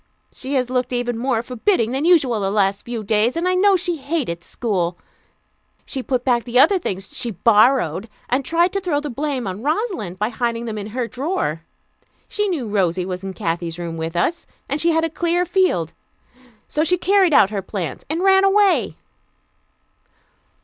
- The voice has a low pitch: No, high, 245 Hz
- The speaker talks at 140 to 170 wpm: No, average, 185 wpm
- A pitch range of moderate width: No, wide, 8.7 semitones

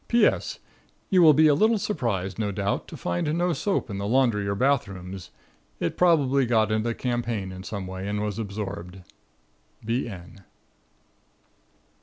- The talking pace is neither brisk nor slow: Yes, average, 160 wpm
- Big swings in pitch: Yes, wide, 5.9 semitones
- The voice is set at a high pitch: No, low, 110 Hz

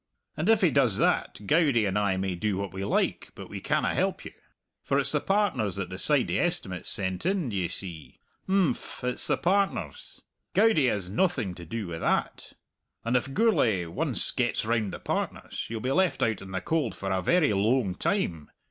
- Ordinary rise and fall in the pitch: No, wide, 8.7 semitones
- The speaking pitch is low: Yes, low, 115 Hz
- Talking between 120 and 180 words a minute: No, average, 195 wpm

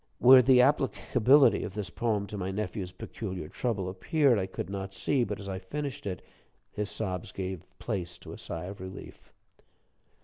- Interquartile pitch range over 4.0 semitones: Yes, average, 4.5 semitones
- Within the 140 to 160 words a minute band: No, average, 175 wpm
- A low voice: Yes, low, 100 Hz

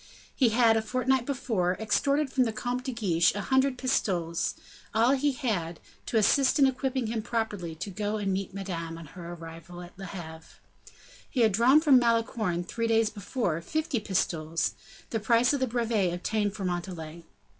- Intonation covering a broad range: Yes, wide, 6.0 semitones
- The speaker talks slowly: No, average, 175 wpm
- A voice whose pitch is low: No, high, 220 Hz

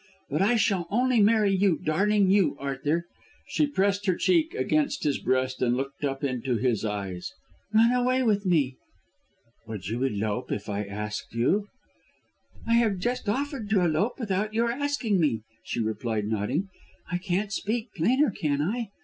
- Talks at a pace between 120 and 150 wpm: No, average, 165 wpm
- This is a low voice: No, medium, 185 Hz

